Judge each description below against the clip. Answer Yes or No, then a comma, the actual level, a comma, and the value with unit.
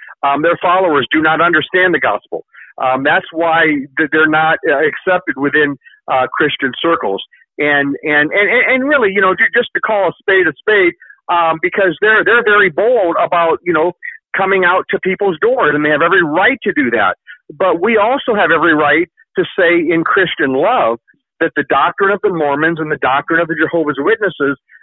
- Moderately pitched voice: Yes, medium, 175 Hz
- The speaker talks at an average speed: Yes, average, 190 wpm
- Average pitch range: No, wide, 6.0 semitones